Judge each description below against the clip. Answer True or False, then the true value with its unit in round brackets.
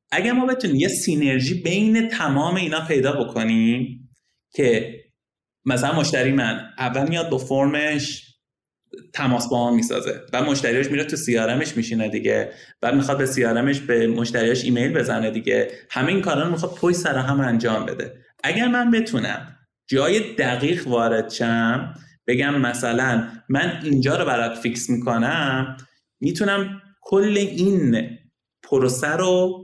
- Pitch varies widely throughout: True (5.7 semitones)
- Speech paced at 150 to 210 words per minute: False (135 wpm)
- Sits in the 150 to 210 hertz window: False (135 Hz)